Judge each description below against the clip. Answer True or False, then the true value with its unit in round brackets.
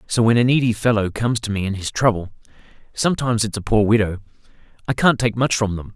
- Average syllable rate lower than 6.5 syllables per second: False (6.6 syllables/s)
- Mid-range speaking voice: False (110 Hz)